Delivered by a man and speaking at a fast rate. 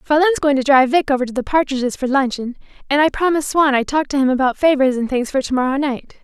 No: female; fast, 250 wpm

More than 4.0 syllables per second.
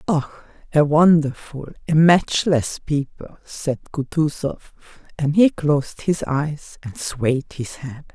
No: 3.7 syllables/s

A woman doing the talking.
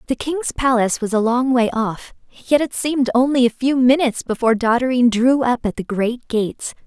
Yes: female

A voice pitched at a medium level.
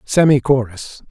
No: low, 130 Hz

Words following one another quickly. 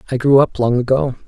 Yes: fast, 235 wpm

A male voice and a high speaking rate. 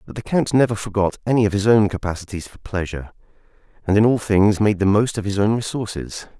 Yes: male; fast, 215 wpm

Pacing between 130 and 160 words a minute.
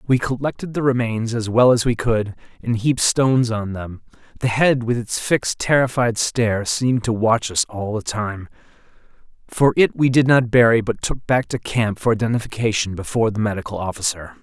No: average, 185 wpm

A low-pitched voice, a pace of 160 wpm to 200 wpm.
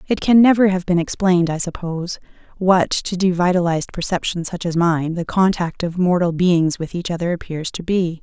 No: medium, 175 Hz; average, 190 wpm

